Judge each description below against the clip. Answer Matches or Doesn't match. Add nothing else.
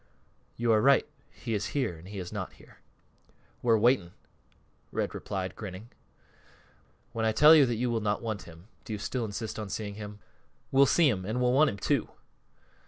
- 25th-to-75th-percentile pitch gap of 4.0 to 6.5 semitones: Doesn't match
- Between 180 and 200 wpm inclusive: Matches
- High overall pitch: Doesn't match